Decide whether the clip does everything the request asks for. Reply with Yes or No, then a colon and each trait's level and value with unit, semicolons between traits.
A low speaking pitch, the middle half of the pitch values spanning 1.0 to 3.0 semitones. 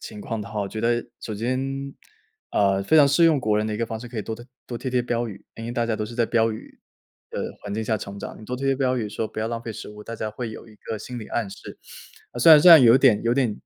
Yes: low, 115 Hz; average, 2.7 semitones